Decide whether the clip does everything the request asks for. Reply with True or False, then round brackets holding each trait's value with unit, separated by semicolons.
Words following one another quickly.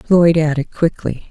False (140 wpm)